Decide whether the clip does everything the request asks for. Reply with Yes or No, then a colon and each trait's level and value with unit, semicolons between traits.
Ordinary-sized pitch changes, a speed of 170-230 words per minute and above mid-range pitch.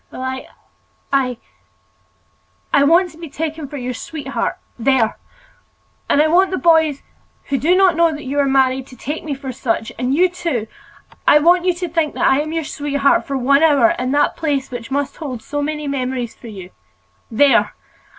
Yes: average, 3.5 semitones; average, 180 wpm; very high, 285 Hz